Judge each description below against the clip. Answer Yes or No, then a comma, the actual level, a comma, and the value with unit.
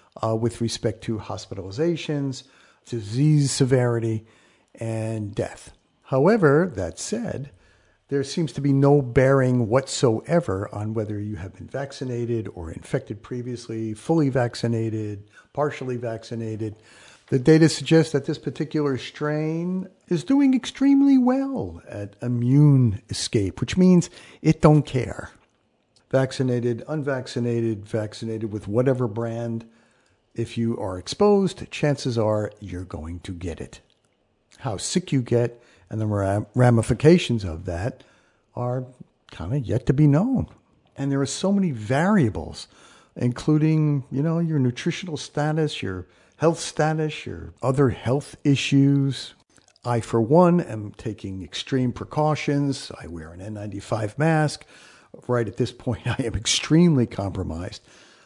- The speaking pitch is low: Yes, low, 125 Hz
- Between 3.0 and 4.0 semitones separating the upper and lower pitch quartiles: No, average, 5.2 semitones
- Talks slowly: Yes, slow, 125 wpm